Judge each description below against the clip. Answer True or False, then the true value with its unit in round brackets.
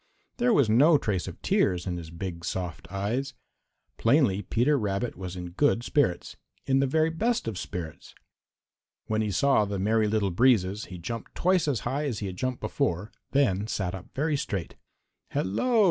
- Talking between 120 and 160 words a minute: False (175 wpm)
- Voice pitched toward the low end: True (110 Hz)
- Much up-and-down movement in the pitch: True (6.7 semitones)